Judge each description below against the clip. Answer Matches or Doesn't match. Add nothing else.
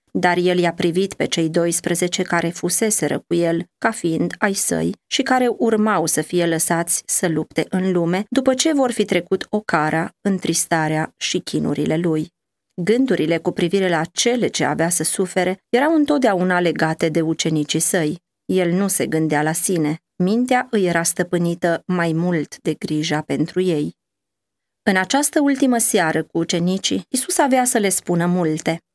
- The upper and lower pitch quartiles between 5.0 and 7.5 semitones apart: Doesn't match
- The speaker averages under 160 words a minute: Doesn't match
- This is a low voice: Doesn't match